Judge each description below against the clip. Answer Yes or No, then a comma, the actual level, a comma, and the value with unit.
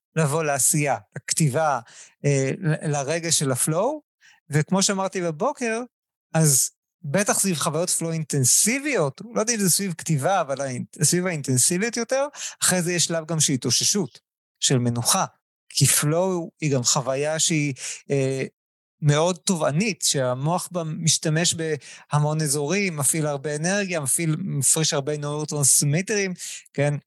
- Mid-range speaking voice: Yes, medium, 160 Hz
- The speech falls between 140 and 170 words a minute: No, average, 125 wpm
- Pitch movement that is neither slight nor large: Yes, average, 4.0 semitones